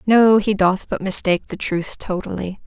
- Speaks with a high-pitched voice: Yes, high, 195 Hz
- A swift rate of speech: No, average, 180 wpm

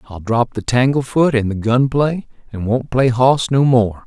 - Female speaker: No, male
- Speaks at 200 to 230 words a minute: Yes, fast, 205 wpm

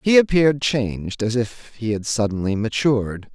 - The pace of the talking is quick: No, average, 160 wpm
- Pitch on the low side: Yes, low, 120 Hz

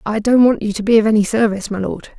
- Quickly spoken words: Yes, fast, 300 wpm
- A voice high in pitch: Yes, high, 215 Hz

